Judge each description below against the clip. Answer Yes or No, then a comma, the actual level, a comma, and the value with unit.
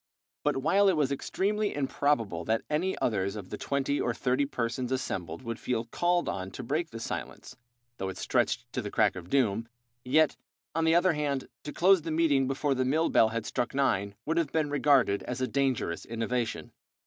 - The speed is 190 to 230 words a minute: Yes, average, 195 wpm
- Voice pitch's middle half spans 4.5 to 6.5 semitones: Yes, average, 4.9 semitones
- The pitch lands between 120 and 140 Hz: Yes, low, 135 Hz